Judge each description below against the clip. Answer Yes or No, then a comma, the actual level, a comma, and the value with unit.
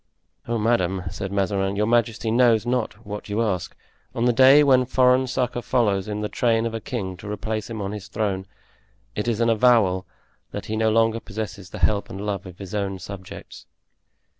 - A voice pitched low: Yes, low, 110 Hz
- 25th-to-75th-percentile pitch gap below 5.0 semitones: Yes, average, 3.1 semitones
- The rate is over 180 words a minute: Yes, average, 195 wpm